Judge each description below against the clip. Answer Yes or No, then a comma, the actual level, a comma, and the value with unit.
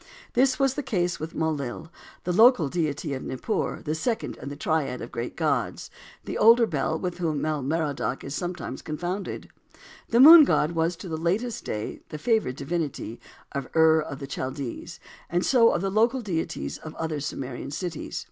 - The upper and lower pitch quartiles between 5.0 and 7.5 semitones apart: Yes, wide, 5.4 semitones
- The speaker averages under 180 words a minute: No, average, 185 wpm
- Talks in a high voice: No, medium, 160 Hz